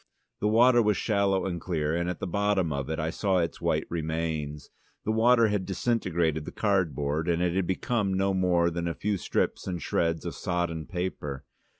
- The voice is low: Yes, very low, 90 Hz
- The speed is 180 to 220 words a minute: Yes, average, 195 wpm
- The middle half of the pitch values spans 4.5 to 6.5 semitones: No, average, 3.6 semitones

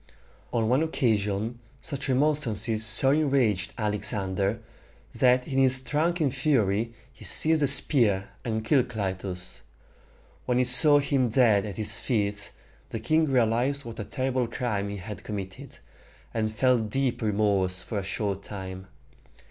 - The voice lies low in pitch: Yes, low, 115 Hz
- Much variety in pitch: No, average, 4.5 semitones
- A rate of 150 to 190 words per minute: No, average, 140 wpm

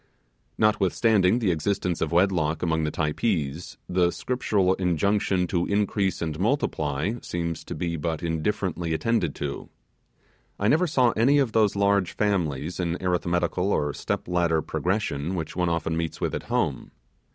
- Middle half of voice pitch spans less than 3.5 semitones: No, average, 3.8 semitones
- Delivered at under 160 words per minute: Yes, average, 150 wpm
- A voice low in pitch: Yes, very low, 90 Hz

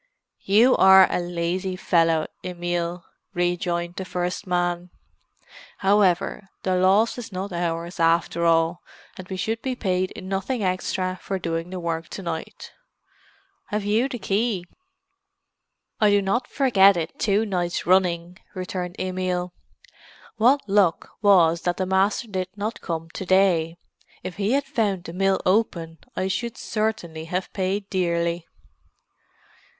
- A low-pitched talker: No, medium, 185 Hz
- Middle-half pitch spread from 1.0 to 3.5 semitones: Yes, narrow, 2.6 semitones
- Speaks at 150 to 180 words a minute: No, average, 140 wpm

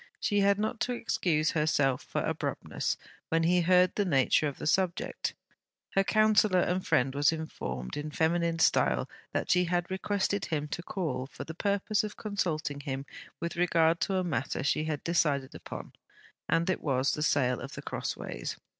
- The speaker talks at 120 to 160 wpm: No, average, 175 wpm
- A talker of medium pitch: Yes, medium, 165 Hz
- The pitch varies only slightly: No, average, 4.5 semitones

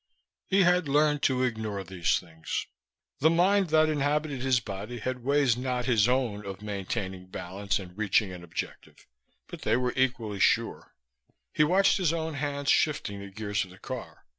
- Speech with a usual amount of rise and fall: No, wide, 6.6 semitones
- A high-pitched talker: No, low, 125 Hz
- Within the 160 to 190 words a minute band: Yes, average, 170 wpm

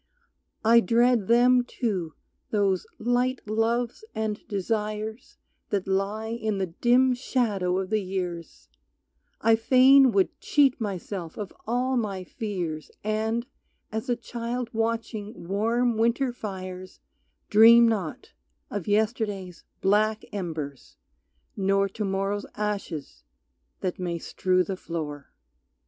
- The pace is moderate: No, slow, 115 wpm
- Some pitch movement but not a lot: Yes, average, 3.6 semitones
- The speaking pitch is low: No, high, 215 Hz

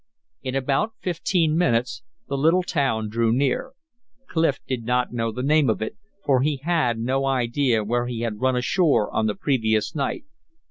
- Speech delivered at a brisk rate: No, average, 175 wpm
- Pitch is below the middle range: Yes, low, 130 Hz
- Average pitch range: Yes, average, 4.1 semitones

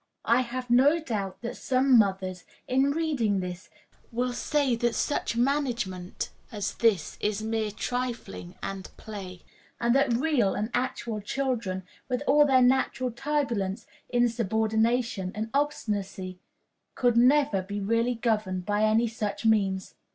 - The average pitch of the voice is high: Yes, high, 230 Hz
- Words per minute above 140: No, slow, 135 wpm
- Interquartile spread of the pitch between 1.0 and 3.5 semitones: No, average, 4.0 semitones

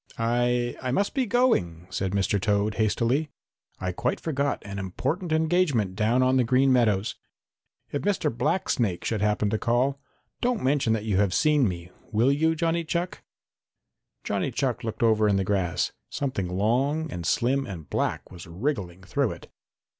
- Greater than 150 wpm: Yes, average, 165 wpm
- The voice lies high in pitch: No, low, 120 Hz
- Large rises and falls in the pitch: Yes, wide, 6.2 semitones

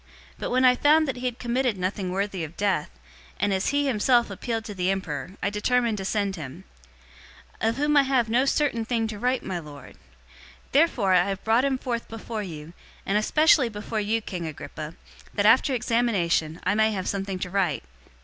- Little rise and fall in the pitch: No, average, 4.8 semitones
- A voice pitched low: No, high, 210 Hz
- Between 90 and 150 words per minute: No, fast, 205 wpm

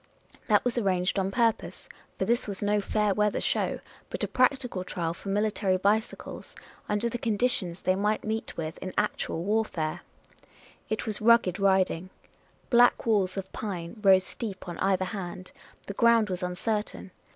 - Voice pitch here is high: Yes, high, 200 Hz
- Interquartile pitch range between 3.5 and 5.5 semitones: No, average, 2.9 semitones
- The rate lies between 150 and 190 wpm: Yes, average, 165 wpm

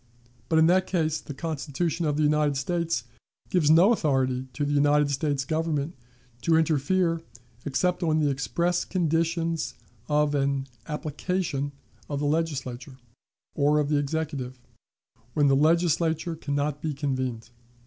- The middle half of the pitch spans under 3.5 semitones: Yes, average, 2.7 semitones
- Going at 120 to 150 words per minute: Yes, average, 140 wpm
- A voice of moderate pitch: Yes, medium, 150 Hz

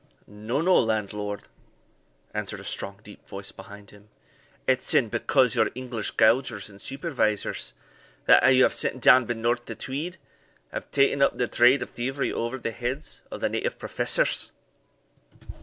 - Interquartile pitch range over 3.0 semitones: Yes, average, 4.0 semitones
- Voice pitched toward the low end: Yes, low, 120 Hz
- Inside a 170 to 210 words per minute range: No, average, 155 wpm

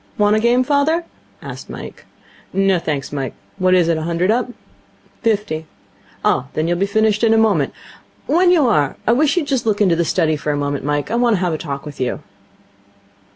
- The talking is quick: Yes, fast, 210 wpm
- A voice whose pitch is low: No, high, 195 Hz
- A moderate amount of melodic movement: No, wide, 6.9 semitones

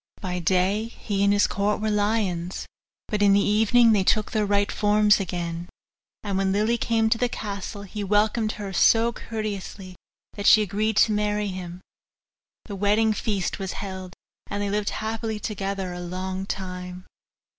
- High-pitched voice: Yes, high, 205 Hz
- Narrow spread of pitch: Yes, narrow, 2.1 semitones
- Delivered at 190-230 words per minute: No, average, 170 wpm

